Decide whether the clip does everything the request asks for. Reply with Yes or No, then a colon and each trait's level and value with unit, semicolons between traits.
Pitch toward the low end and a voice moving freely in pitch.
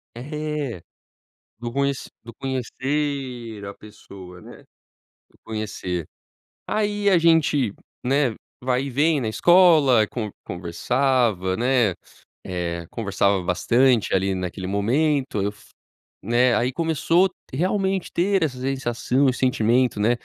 Yes: low, 125 Hz; wide, 5.7 semitones